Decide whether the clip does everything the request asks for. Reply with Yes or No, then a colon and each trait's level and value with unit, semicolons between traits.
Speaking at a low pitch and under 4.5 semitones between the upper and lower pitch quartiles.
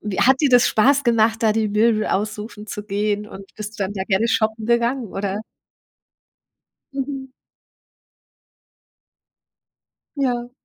No: high, 220 Hz; narrow, 2.5 semitones